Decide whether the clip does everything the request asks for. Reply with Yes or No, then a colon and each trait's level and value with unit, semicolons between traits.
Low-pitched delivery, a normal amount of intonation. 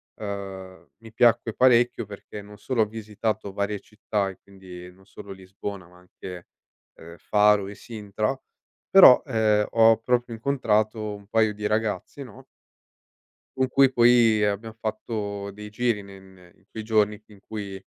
No: low, 105 Hz; narrow, 2.2 semitones